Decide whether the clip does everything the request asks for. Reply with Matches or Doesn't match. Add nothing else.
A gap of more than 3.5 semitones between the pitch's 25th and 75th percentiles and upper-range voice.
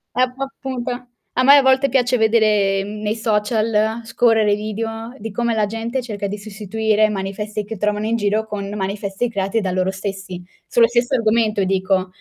Doesn't match